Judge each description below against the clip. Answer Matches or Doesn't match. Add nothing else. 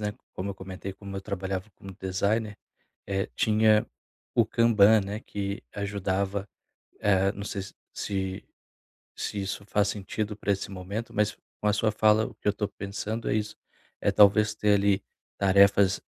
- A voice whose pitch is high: Doesn't match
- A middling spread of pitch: Doesn't match